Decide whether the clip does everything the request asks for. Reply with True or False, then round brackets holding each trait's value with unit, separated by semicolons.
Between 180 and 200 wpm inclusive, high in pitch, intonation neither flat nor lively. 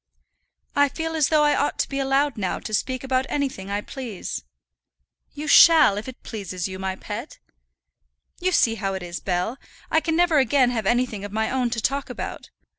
False (195 wpm; 255 Hz; 5.8 semitones)